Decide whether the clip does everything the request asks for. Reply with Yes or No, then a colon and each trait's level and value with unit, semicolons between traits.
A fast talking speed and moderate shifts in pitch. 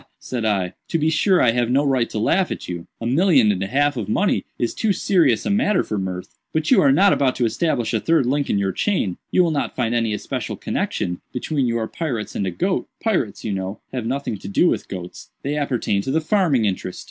No: fast, 225 wpm; wide, 7.0 semitones